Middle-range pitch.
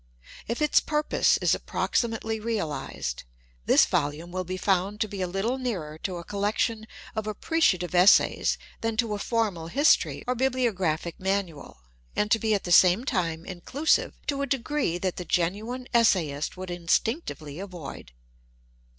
No: high, 200 Hz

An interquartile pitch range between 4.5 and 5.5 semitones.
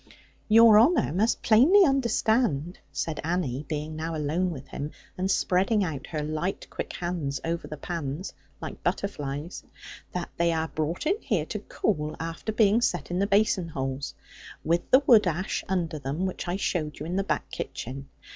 Yes: average, 5.0 semitones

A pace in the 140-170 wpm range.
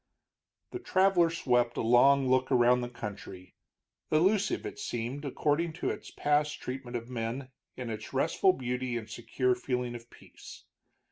Yes: average, 150 wpm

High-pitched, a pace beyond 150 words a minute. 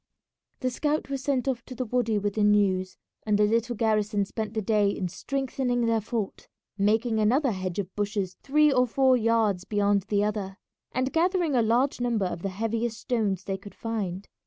Yes: high, 220 Hz; average, 190 wpm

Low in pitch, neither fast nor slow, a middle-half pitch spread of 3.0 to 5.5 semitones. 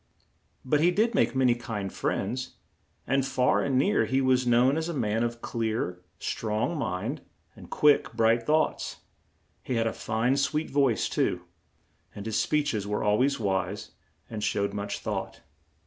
Yes: low, 120 Hz; average, 170 wpm; average, 4.3 semitones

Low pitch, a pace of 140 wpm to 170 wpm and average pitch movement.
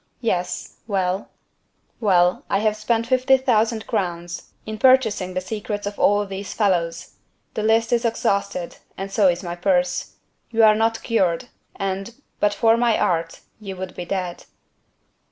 No: high, 205 Hz; average, 155 wpm; average, 3.7 semitones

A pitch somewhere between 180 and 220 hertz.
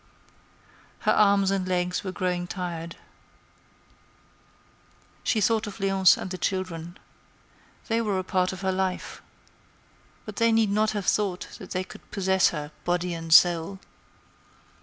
Yes: medium, 185 Hz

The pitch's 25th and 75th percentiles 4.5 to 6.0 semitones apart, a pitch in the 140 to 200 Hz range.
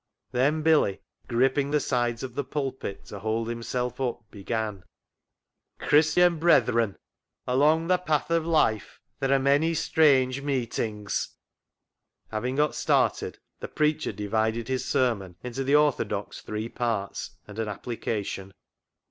No: average, 5.0 semitones; low, 125 Hz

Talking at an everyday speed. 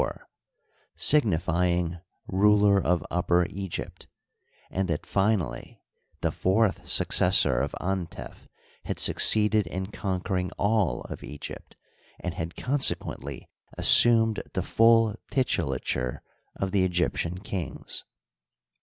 No: slow, 105 wpm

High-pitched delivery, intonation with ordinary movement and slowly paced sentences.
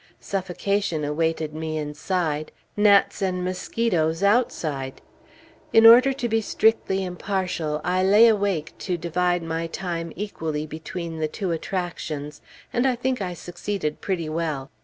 No: medium, 175 Hz; average, 4.0 semitones; slow, 130 wpm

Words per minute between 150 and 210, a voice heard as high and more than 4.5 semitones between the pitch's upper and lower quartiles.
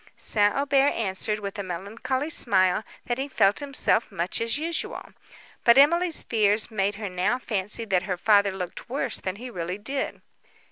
Yes: average, 170 wpm; high, 210 Hz; average, 5.2 semitones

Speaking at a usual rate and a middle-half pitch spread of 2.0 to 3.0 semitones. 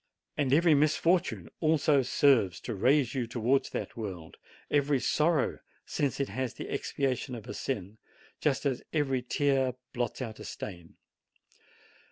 No: average, 145 wpm; average, 3.9 semitones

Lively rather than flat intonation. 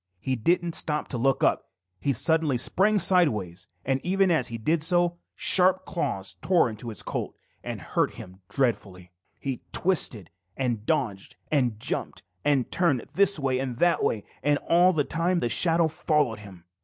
Yes: wide, 6.9 semitones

